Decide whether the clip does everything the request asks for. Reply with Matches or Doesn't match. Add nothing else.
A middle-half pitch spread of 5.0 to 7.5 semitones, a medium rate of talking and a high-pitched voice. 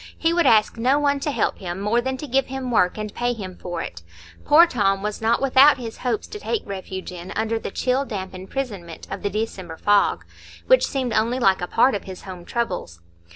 Doesn't match